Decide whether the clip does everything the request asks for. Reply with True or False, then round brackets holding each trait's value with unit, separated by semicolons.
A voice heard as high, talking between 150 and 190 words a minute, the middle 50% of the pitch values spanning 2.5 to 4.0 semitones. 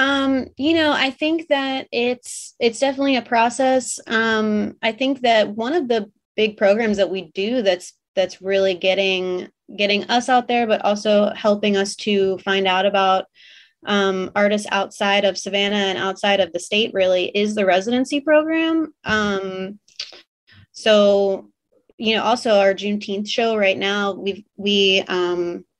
True (205 Hz; 155 wpm; 3.7 semitones)